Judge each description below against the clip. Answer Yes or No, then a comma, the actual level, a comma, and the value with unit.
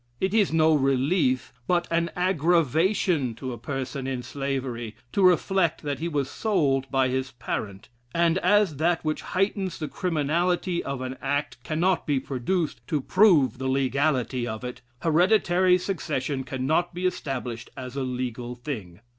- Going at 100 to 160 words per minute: Yes, average, 155 wpm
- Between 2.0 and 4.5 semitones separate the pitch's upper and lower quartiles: No, average, 5.2 semitones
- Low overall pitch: No, medium, 145 Hz